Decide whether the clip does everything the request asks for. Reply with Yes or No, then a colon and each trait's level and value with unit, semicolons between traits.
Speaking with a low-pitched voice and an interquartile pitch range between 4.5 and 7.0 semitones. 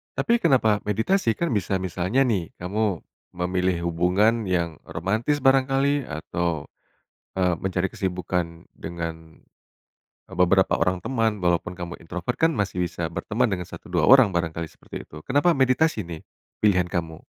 Yes: very low, 95 Hz; average, 5.2 semitones